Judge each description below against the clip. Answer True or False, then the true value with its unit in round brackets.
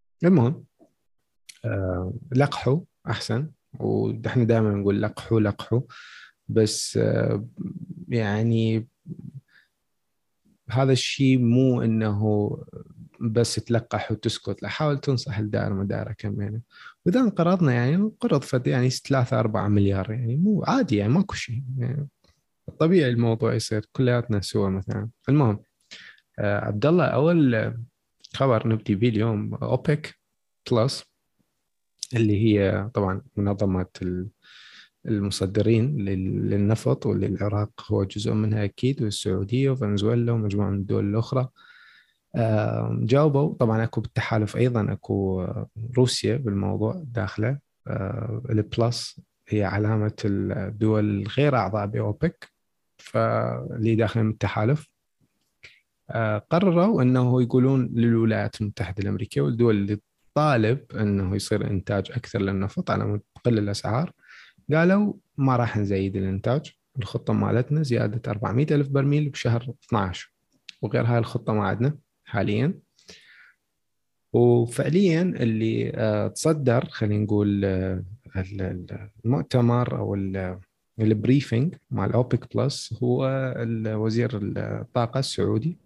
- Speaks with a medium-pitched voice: False (115 Hz)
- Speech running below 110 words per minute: True (100 wpm)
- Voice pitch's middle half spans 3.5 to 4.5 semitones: True (4.0 semitones)